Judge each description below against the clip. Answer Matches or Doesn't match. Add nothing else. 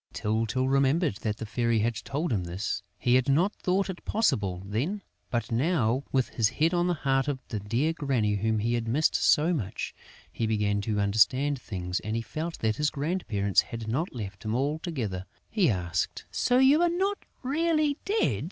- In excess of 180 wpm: Matches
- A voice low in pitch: Matches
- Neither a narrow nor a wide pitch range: Doesn't match